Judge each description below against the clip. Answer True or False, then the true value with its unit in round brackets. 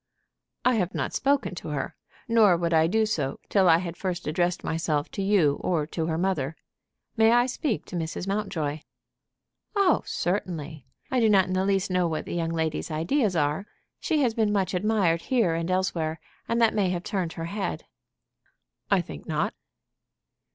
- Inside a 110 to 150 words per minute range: False (180 wpm)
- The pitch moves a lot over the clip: False (4.3 semitones)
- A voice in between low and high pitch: True (180 Hz)